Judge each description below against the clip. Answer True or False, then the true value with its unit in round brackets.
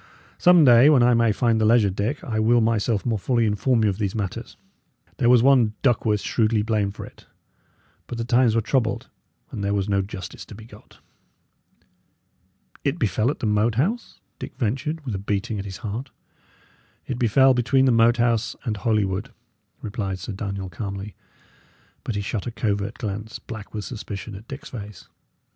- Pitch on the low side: True (110 Hz)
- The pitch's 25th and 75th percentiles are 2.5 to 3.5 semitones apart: True (3.0 semitones)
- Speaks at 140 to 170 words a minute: False (185 wpm)